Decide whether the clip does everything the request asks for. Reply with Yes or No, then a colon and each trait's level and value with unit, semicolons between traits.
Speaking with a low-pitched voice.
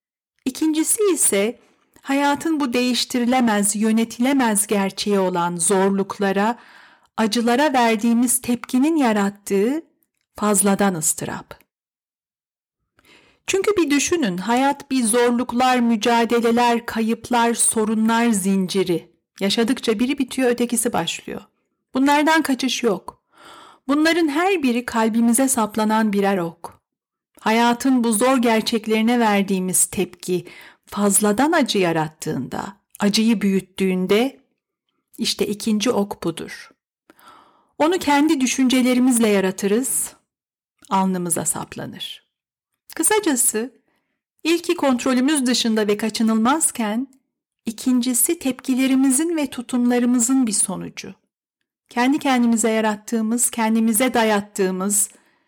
No: high, 235 Hz